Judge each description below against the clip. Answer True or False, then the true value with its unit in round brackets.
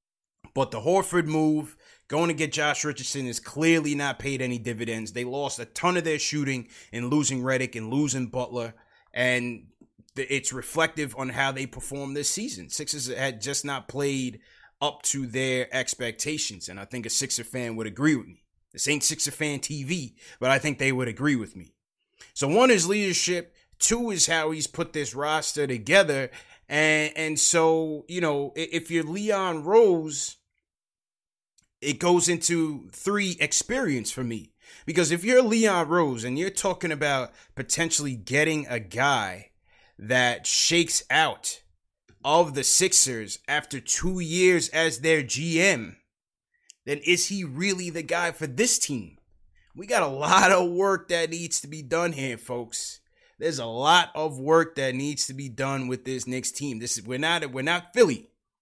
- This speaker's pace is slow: False (170 wpm)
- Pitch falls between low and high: True (145 Hz)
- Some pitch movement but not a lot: True (4.6 semitones)